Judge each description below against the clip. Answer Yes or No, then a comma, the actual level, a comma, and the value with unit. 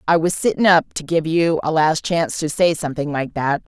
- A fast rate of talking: Yes, fast, 240 wpm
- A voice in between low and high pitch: Yes, medium, 160 Hz